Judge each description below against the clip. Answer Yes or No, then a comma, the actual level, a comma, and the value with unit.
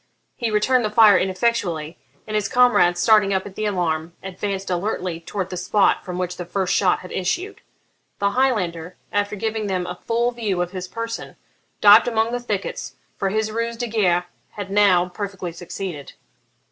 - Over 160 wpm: Yes, average, 175 wpm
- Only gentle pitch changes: No, average, 3.4 semitones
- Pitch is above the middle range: Yes, high, 200 Hz